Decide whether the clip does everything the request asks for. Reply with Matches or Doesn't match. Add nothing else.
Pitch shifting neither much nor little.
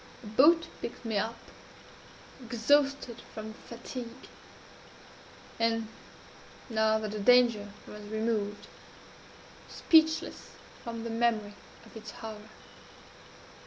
Doesn't match